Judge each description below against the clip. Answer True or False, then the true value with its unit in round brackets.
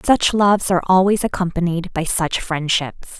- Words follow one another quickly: False (150 wpm)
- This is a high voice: False (180 Hz)